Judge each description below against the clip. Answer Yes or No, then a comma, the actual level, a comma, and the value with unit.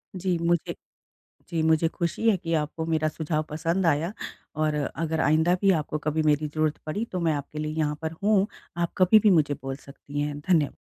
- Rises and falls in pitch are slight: Yes, narrow, 2.2 semitones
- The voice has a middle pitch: Yes, medium, 160 Hz